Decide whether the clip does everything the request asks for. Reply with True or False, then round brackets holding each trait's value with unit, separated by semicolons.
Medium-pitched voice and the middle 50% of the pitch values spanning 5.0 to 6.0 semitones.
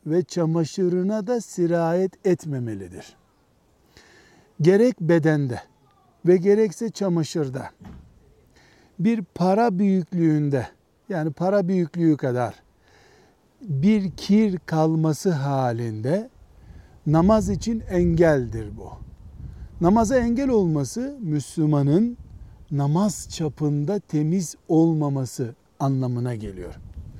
True (165 Hz; 5.4 semitones)